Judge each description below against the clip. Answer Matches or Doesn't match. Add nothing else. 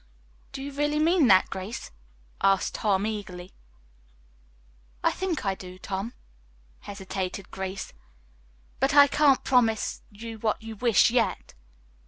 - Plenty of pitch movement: Matches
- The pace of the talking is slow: Matches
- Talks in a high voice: Matches